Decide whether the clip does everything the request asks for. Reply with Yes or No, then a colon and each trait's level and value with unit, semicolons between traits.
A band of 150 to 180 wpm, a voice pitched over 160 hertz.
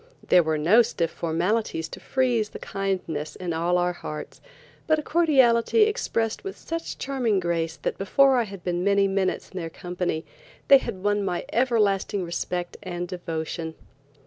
Yes: average, 165 wpm; high, 190 Hz